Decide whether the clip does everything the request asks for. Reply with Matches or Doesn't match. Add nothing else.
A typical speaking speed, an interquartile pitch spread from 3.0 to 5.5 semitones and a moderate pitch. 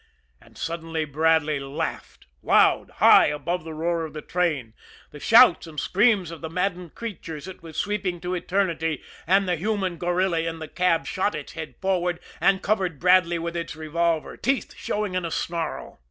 Doesn't match